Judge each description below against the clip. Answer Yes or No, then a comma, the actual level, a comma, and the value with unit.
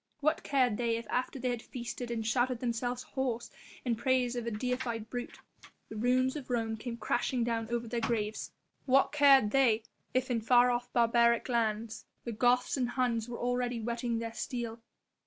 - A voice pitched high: Yes, high, 240 Hz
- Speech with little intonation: Yes, narrow, 1.5 semitones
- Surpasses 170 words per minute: Yes, average, 180 wpm